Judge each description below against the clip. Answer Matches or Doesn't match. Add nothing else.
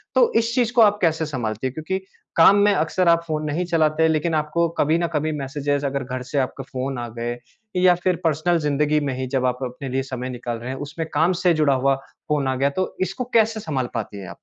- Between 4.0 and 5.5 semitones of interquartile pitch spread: Matches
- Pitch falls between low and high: Matches